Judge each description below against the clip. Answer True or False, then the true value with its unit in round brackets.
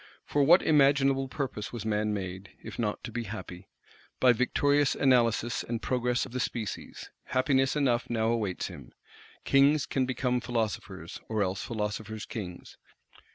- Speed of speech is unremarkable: True (150 wpm)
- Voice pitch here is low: True (120 Hz)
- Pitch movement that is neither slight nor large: True (4.0 semitones)